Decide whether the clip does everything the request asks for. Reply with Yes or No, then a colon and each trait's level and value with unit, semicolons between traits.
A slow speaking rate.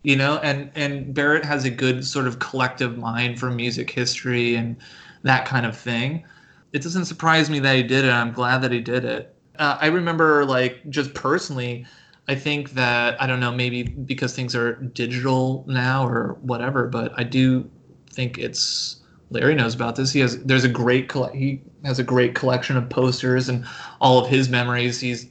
No: average, 195 wpm